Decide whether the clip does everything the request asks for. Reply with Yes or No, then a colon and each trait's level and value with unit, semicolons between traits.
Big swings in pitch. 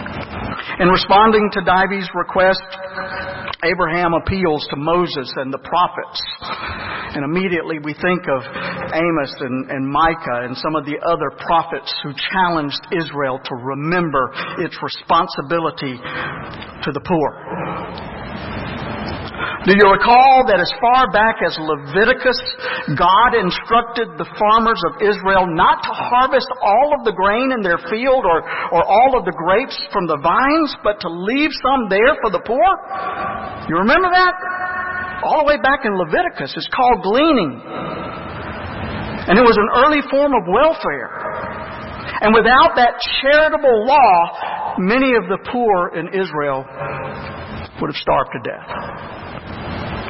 Yes: wide, 7.3 semitones